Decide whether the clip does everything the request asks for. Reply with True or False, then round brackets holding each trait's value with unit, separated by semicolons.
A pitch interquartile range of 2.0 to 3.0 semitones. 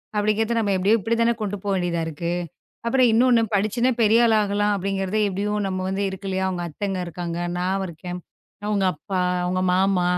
True (2.7 semitones)